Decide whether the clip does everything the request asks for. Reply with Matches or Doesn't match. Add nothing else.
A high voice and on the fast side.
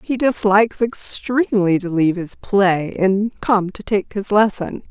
Doesn't match